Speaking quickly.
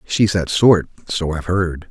No: average, 155 wpm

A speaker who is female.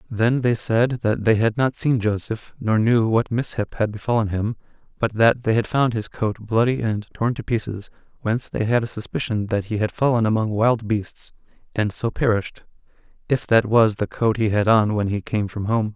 No: male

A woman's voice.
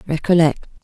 Yes: female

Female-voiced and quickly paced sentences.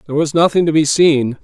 No: male; fast, 250 wpm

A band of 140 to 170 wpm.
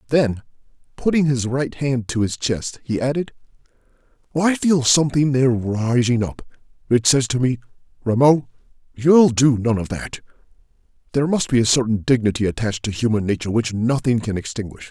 Yes: average, 155 wpm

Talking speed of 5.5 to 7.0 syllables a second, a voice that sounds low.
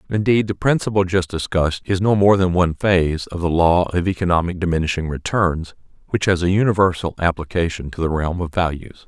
Yes: 5.8 syllables/s; very low, 90 Hz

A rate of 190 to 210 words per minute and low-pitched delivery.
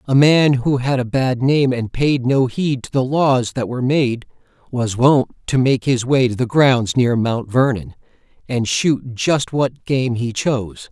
Yes: fast, 205 wpm; low, 130 Hz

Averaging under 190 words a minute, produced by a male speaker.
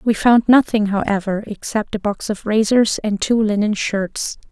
No: average, 175 wpm; female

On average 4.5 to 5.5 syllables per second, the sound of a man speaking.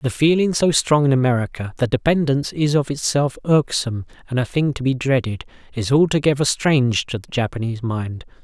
No: 5.7 syllables/s; male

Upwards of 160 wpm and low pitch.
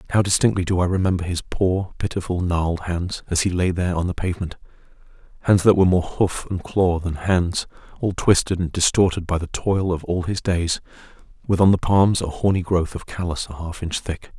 Yes: fast, 205 wpm; very low, 90 Hz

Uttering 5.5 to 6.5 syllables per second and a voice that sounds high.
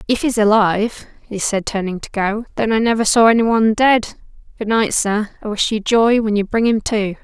No: 5.3 syllables/s; high, 215 Hz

